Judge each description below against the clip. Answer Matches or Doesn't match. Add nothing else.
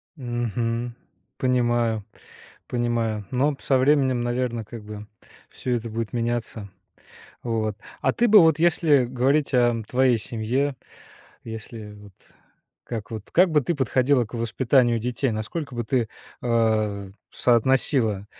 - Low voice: Matches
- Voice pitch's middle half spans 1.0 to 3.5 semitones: Matches